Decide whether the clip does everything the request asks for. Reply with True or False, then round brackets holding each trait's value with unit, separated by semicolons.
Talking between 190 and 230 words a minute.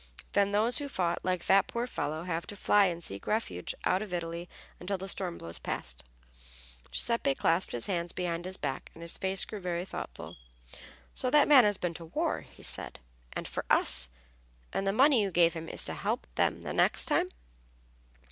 True (200 wpm)